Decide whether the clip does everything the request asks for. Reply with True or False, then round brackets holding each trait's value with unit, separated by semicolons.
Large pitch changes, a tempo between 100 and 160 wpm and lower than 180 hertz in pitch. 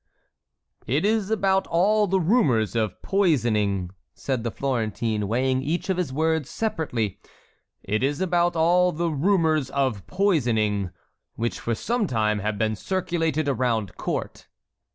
True (8.2 semitones; 135 wpm; 140 Hz)